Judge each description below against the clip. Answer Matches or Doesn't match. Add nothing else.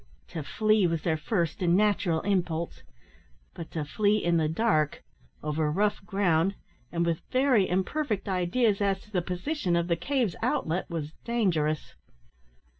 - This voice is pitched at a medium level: Matches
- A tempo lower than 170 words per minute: Matches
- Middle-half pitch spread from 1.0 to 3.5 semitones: Doesn't match